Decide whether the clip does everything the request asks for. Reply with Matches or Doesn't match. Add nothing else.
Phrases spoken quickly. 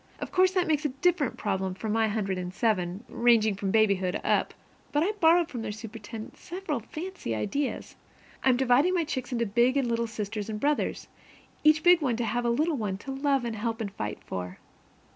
Matches